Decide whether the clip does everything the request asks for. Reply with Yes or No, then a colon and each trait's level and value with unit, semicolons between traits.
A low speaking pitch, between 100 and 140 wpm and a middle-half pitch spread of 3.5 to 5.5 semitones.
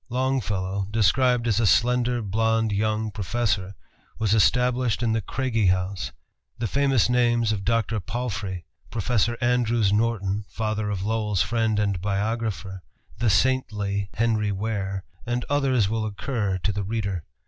No: low, 110 Hz; slow, 135 wpm; average, 3.0 semitones